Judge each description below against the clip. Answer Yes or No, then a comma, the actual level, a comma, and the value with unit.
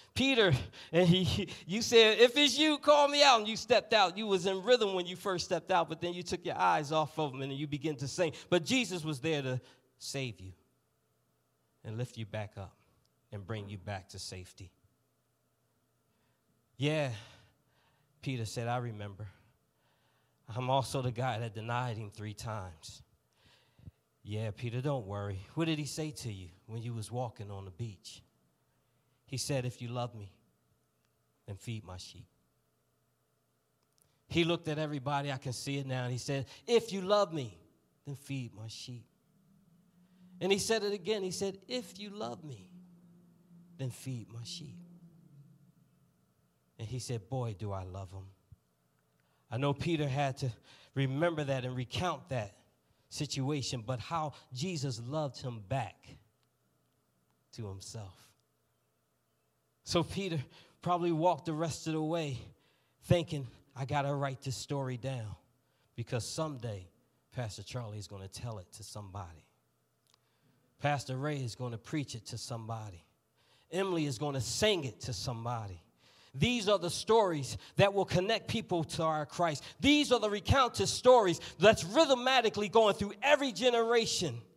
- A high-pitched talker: No, low, 135 Hz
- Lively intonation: Yes, wide, 7.7 semitones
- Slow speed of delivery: No, average, 160 wpm